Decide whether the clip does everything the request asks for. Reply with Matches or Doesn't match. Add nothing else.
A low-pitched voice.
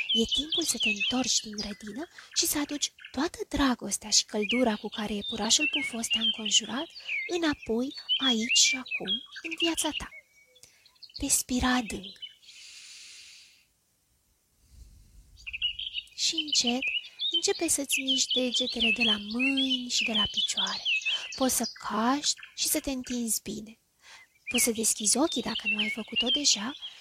Doesn't match